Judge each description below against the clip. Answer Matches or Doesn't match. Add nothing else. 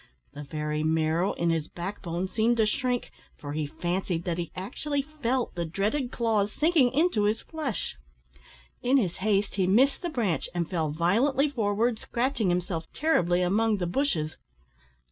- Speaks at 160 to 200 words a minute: Matches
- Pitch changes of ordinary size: Doesn't match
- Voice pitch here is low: Doesn't match